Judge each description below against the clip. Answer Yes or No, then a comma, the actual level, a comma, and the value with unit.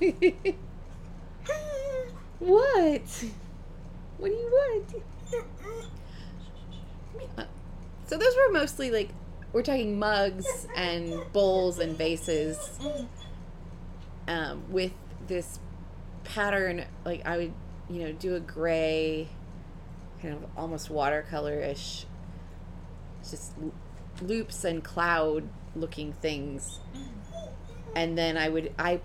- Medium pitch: Yes, medium, 160 Hz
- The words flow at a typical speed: No, slow, 95 wpm